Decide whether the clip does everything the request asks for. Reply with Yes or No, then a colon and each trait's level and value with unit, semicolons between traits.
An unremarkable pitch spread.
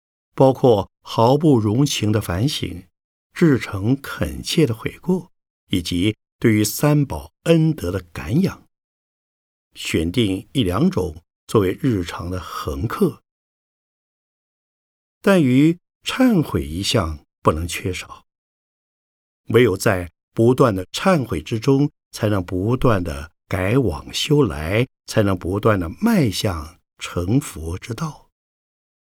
No: wide, 7.6 semitones